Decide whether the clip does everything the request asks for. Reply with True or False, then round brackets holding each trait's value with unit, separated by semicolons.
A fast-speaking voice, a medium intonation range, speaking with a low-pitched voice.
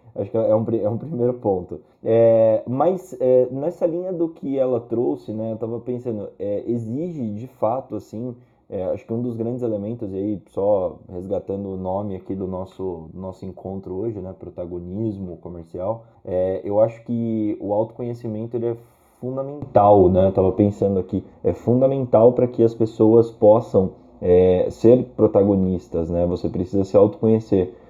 False (160 wpm; 3.9 semitones; 110 Hz)